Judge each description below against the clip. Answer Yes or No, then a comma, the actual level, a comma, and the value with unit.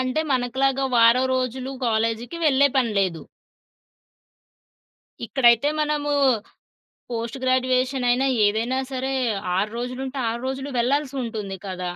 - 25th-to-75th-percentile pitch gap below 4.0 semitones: Yes, narrow, 2.6 semitones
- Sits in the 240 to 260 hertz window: Yes, very high, 255 Hz